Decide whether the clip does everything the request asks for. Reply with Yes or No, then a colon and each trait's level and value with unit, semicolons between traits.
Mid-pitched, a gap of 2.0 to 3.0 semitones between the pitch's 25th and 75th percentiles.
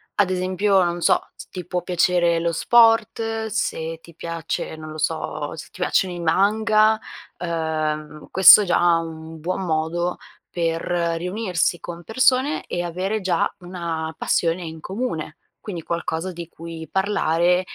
Yes: medium, 175 Hz; average, 2.7 semitones